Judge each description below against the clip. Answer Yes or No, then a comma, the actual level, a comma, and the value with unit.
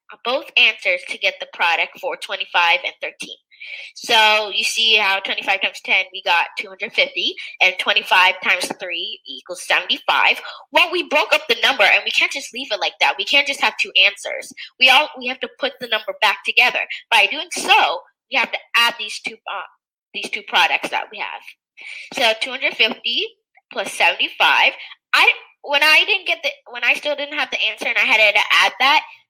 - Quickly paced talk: Yes, fast, 215 wpm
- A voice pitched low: No, very high, 255 Hz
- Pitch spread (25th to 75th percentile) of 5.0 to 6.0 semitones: Yes, wide, 5.4 semitones